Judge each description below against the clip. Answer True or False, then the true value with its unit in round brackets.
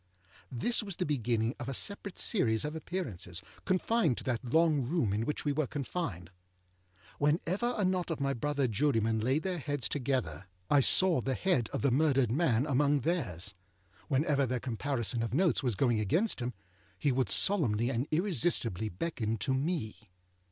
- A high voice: False (135 Hz)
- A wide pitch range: True (5.9 semitones)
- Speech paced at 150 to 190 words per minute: True (170 wpm)